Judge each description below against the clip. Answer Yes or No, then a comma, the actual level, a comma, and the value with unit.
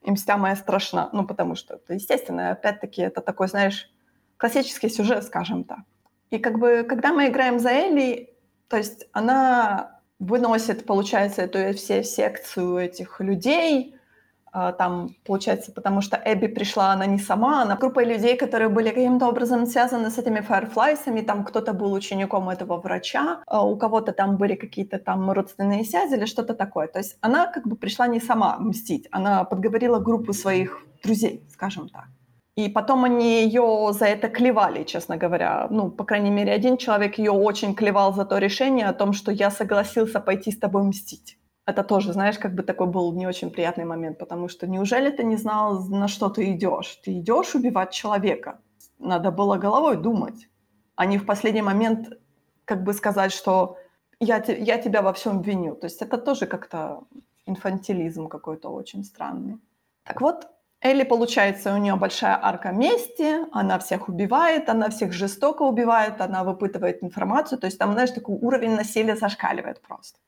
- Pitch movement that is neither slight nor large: Yes, average, 3.5 semitones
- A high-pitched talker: Yes, high, 210 Hz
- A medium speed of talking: No, fast, 170 wpm